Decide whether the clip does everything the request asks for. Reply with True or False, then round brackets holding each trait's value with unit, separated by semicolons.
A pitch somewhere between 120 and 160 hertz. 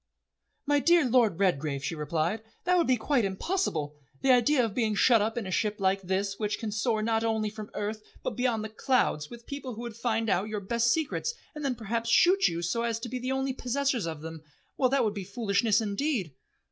False (225 Hz)